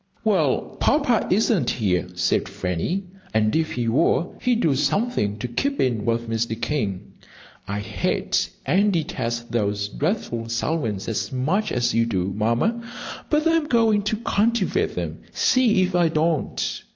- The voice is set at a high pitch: No, low, 135 Hz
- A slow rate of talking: No, average, 150 wpm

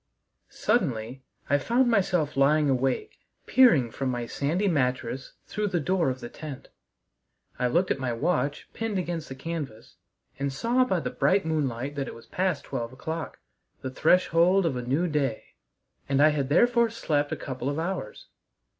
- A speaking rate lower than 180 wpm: Yes, average, 170 wpm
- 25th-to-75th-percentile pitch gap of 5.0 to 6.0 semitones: Yes, wide, 5.6 semitones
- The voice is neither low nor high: Yes, medium, 150 Hz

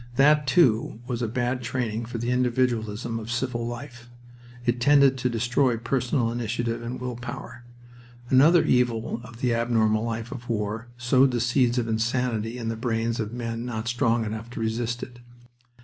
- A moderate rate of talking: Yes, average, 165 wpm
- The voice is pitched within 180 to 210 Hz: No, low, 120 Hz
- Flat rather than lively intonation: Yes, narrow, 1.5 semitones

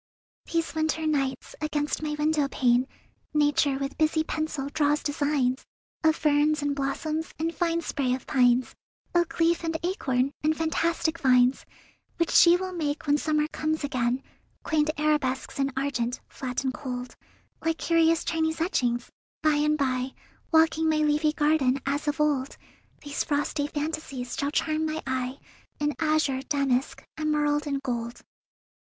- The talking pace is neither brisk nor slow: Yes, average, 150 wpm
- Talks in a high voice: Yes, very high, 295 Hz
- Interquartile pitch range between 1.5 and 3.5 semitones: Yes, average, 2.7 semitones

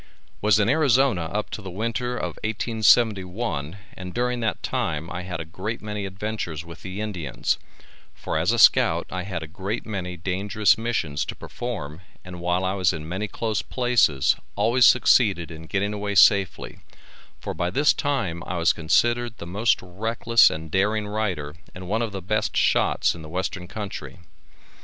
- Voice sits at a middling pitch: No, low, 100 Hz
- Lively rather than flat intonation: No, average, 4.1 semitones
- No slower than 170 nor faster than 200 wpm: Yes, average, 175 wpm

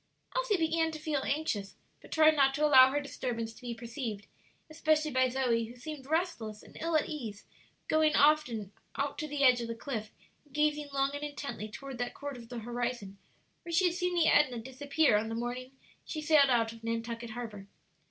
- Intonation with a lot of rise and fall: No, average, 4.7 semitones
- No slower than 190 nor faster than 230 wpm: Yes, average, 200 wpm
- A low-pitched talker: No, very high, 270 Hz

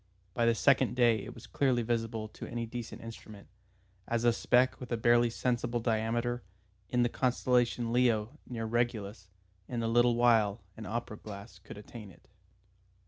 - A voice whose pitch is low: Yes, low, 115 Hz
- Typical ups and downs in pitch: No, narrow, 1.5 semitones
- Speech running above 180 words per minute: No, average, 165 wpm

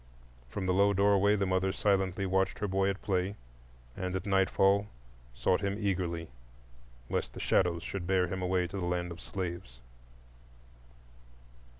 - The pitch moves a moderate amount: No, narrow, 1.6 semitones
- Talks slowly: No, average, 150 wpm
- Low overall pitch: Yes, very low, 95 Hz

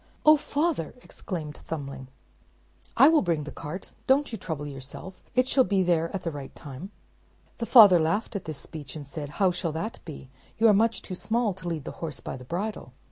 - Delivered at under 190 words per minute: No, fast, 205 wpm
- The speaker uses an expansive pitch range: Yes, wide, 6.5 semitones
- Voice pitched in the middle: Yes, medium, 175 Hz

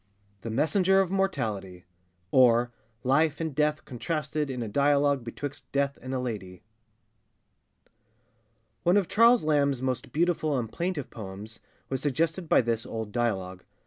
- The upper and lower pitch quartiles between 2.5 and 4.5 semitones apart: No, average, 5.1 semitones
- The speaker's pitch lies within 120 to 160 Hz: Yes, low, 135 Hz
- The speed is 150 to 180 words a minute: No, average, 140 wpm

